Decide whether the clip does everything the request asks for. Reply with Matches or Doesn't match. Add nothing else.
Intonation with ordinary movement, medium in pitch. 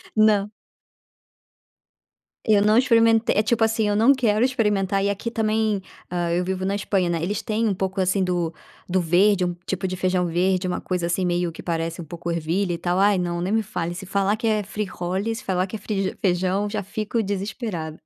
Doesn't match